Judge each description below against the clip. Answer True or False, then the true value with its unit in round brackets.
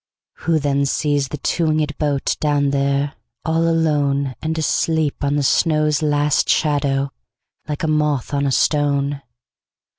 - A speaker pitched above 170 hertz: False (145 Hz)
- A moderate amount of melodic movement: False (1.6 semitones)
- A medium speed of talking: False (125 wpm)